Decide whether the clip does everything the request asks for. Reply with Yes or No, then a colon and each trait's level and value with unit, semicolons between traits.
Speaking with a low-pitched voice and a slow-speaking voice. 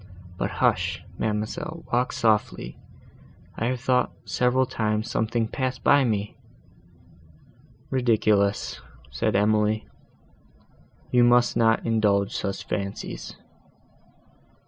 Yes: low, 110 Hz; slow, 95 wpm